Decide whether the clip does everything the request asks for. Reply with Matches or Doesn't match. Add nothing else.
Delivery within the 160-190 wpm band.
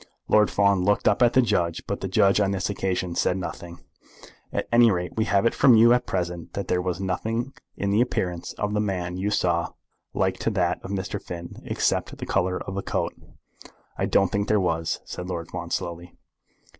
Doesn't match